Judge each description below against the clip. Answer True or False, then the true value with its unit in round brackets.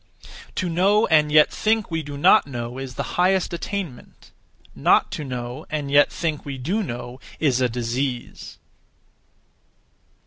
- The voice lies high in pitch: False (145 Hz)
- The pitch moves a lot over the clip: True (5.7 semitones)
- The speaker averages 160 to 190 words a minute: False (145 wpm)